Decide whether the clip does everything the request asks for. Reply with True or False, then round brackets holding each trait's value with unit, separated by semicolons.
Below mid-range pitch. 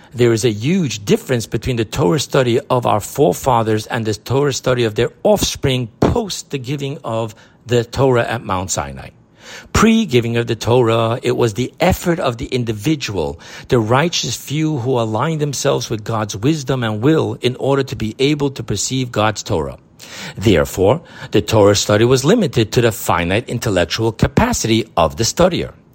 True (120 Hz)